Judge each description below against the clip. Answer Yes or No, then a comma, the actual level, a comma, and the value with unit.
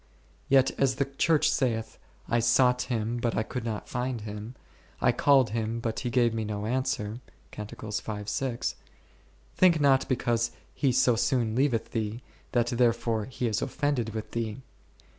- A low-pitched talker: Yes, low, 120 Hz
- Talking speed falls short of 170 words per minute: Yes, average, 160 wpm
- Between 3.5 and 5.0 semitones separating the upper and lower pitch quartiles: No, average, 2.8 semitones